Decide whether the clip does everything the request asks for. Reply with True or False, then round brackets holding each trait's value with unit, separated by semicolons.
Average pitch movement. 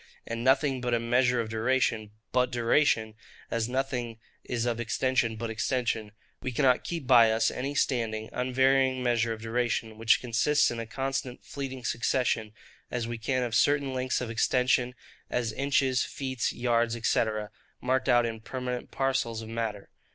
False (2.2 semitones)